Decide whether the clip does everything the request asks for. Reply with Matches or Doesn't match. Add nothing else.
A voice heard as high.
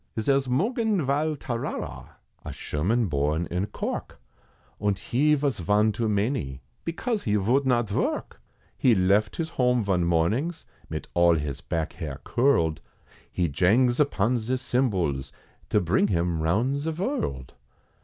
Doesn't match